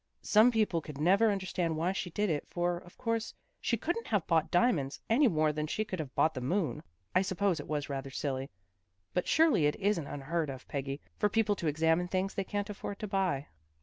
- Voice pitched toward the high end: No, medium, 175 Hz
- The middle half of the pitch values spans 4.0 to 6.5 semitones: Yes, average, 5.3 semitones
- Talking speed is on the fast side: Yes, fast, 215 wpm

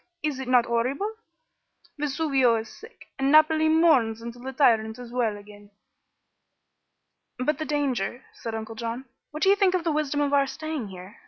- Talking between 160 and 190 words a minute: Yes, average, 175 wpm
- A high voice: Yes, very high, 265 Hz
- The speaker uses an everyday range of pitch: Yes, average, 5.0 semitones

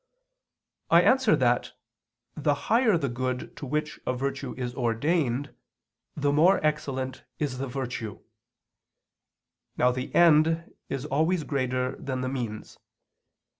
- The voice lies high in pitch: No, low, 135 Hz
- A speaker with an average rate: No, slow, 125 wpm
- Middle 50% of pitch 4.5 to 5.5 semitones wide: No, average, 3.3 semitones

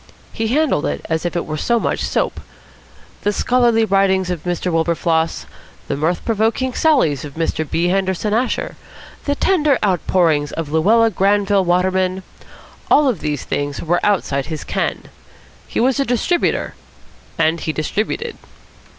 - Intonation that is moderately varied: No, wide, 5.9 semitones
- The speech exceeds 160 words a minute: No, average, 145 wpm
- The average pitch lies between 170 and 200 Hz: Yes, high, 190 Hz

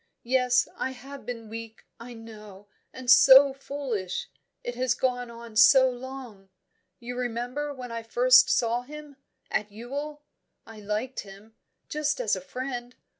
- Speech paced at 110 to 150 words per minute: Yes, average, 145 wpm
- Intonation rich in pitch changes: No, narrow, 2.6 semitones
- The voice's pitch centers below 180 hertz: No, high, 245 Hz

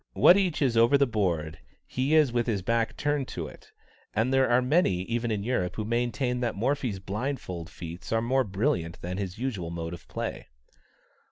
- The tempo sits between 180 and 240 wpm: Yes, average, 190 wpm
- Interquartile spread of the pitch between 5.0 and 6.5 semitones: Yes, wide, 5.6 semitones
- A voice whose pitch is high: No, low, 115 Hz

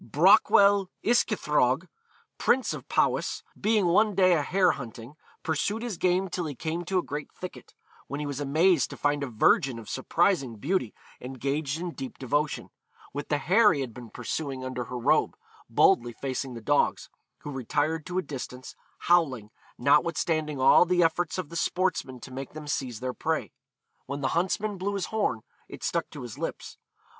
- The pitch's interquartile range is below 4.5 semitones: No, wide, 5.6 semitones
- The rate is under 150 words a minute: No, average, 175 wpm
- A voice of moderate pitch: Yes, medium, 150 Hz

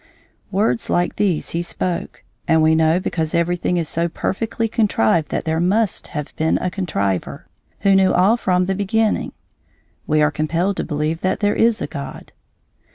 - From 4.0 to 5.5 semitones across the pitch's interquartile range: No, average, 3.6 semitones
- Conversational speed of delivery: Yes, average, 170 wpm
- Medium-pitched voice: Yes, medium, 175 Hz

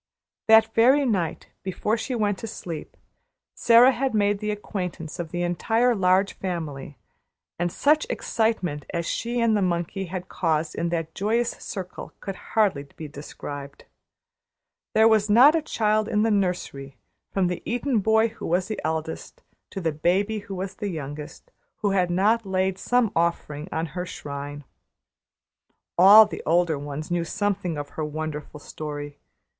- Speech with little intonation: No, wide, 5.4 semitones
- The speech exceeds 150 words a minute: Yes, average, 160 wpm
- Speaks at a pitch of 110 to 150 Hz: No, medium, 185 Hz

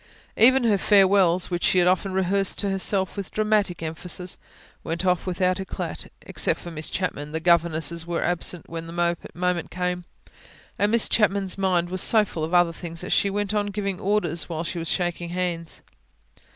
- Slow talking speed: No, average, 180 wpm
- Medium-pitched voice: Yes, medium, 180 Hz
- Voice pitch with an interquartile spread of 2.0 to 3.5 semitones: Yes, narrow, 2.5 semitones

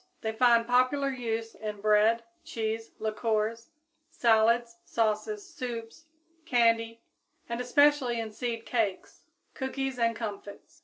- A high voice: Yes, high, 230 Hz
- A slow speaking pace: Yes, slow, 110 wpm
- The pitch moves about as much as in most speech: No, narrow, 2.2 semitones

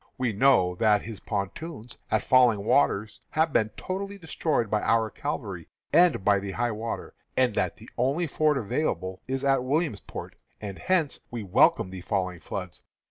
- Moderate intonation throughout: No, wide, 6.3 semitones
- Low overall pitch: Yes, low, 120 Hz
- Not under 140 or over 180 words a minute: Yes, average, 165 wpm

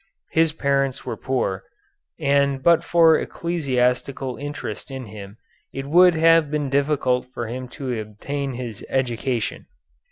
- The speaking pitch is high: No, low, 135 Hz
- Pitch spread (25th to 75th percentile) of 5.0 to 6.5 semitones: No, average, 2.9 semitones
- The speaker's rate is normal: No, slow, 130 wpm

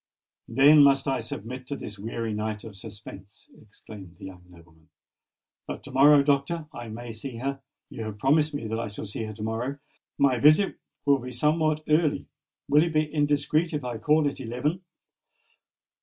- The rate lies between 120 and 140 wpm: No, average, 175 wpm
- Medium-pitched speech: No, low, 130 Hz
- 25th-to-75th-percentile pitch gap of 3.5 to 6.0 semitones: Yes, average, 5.2 semitones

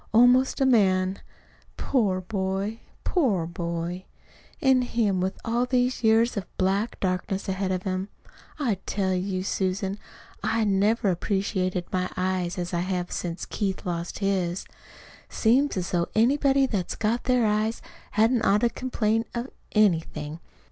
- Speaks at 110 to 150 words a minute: Yes, average, 140 wpm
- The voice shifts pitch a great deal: No, average, 3.8 semitones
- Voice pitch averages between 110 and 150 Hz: No, high, 195 Hz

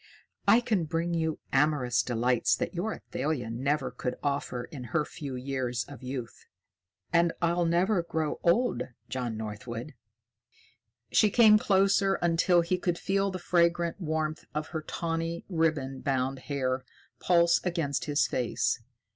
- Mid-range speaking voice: Yes, medium, 155 Hz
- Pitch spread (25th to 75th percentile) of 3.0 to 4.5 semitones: No, average, 4.9 semitones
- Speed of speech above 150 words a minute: No, average, 140 wpm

